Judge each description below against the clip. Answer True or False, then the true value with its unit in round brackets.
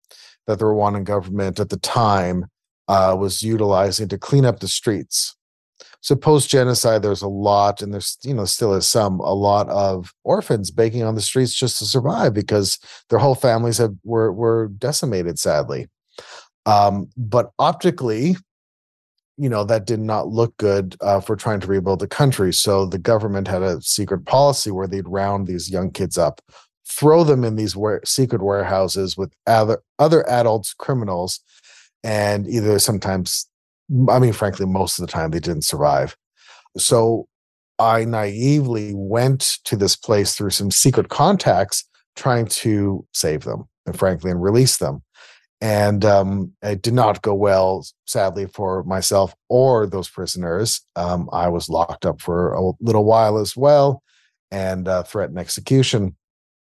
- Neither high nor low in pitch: False (105 Hz)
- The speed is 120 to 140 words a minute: False (160 wpm)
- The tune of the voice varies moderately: True (3.4 semitones)